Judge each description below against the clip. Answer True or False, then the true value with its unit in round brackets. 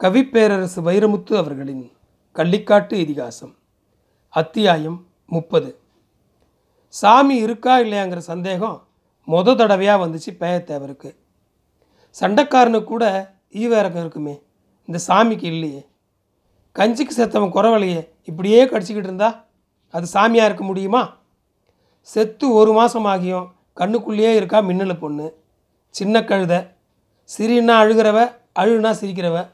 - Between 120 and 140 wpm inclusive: False (95 wpm)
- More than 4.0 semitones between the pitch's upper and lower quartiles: True (5.4 semitones)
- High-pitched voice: True (195 Hz)